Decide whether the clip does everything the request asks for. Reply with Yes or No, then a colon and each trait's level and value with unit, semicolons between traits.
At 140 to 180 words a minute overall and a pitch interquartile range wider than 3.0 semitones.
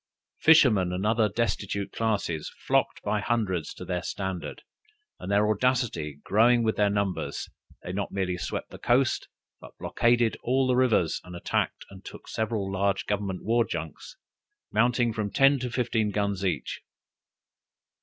Yes: average, 150 wpm; average, 3.7 semitones